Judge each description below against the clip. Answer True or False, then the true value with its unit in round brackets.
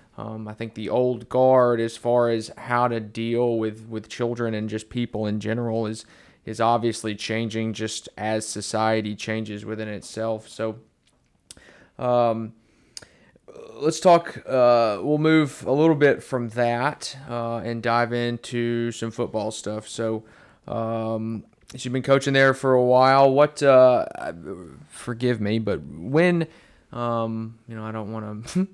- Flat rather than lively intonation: True (2.2 semitones)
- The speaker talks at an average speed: True (150 wpm)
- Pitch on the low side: True (115 Hz)